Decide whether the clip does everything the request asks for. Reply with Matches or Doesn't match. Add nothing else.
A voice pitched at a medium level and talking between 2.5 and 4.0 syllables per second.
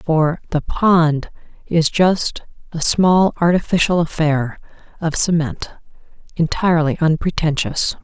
Matches